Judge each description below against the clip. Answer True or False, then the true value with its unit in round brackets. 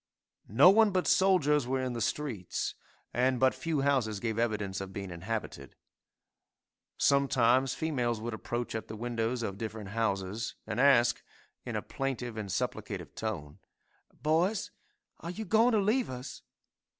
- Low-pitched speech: True (120 Hz)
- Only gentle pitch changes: False (4.8 semitones)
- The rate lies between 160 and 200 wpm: False (150 wpm)